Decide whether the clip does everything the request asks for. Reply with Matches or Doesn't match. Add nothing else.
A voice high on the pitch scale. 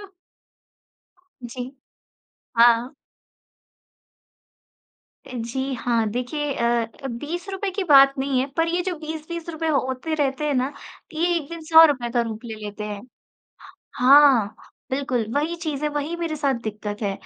Matches